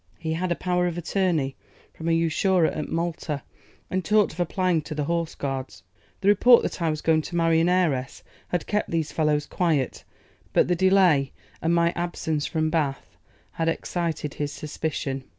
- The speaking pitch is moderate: Yes, medium, 165 Hz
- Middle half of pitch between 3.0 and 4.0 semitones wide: No, narrow, 2.6 semitones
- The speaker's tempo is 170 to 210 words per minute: Yes, average, 180 wpm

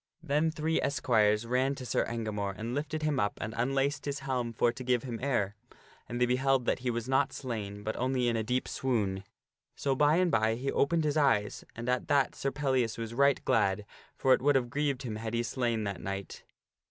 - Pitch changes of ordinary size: Yes, average, 3.5 semitones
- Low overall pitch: Yes, low, 125 Hz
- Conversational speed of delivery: No, fast, 215 wpm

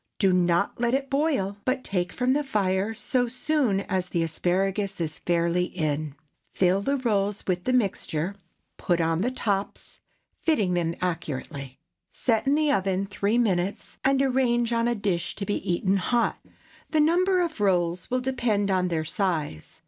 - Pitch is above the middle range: Yes, high, 195 Hz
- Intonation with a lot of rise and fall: Yes, wide, 5.8 semitones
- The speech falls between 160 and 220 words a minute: Yes, average, 165 wpm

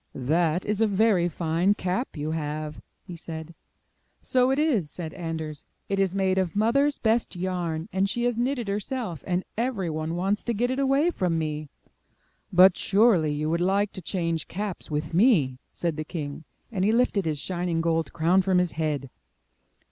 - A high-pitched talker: No, medium, 180 Hz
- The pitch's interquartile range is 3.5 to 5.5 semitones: Yes, average, 4.6 semitones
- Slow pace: No, average, 185 wpm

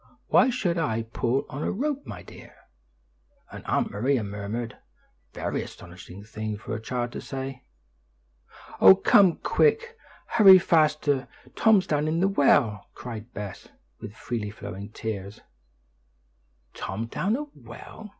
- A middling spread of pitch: No, wide, 9.0 semitones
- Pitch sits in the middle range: No, low, 125 Hz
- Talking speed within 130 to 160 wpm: Yes, slow, 135 wpm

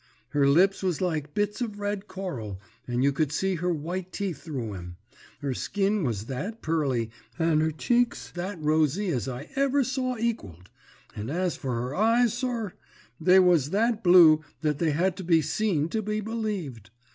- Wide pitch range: Yes, wide, 6.4 semitones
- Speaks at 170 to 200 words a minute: Yes, average, 180 wpm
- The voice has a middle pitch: Yes, medium, 175 Hz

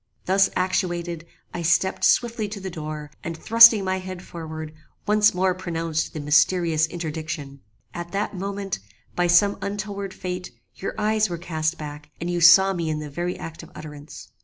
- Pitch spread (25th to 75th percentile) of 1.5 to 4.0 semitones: Yes, average, 3.3 semitones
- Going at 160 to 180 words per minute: Yes, average, 170 wpm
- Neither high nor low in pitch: Yes, medium, 175 Hz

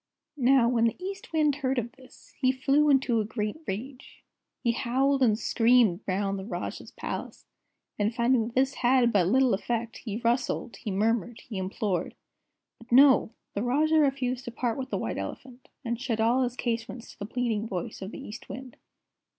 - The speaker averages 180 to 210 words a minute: Yes, average, 185 wpm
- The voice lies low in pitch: No, high, 240 Hz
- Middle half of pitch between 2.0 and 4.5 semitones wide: Yes, average, 2.9 semitones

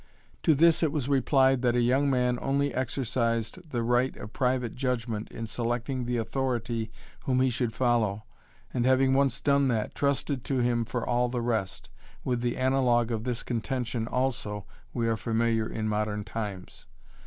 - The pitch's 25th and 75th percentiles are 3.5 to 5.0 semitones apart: No, narrow, 2.4 semitones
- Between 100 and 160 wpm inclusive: No, average, 170 wpm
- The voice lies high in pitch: No, low, 120 Hz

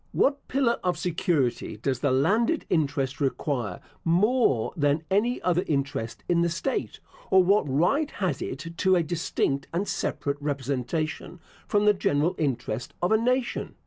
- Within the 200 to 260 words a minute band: No, average, 150 wpm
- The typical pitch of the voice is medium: Yes, medium, 165 Hz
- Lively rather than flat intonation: Yes, wide, 6.1 semitones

